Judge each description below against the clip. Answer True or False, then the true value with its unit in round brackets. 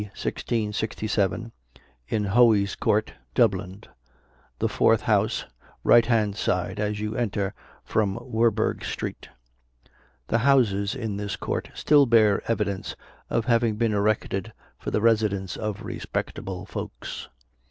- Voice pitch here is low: True (105 Hz)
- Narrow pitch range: True (2.3 semitones)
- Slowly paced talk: True (120 wpm)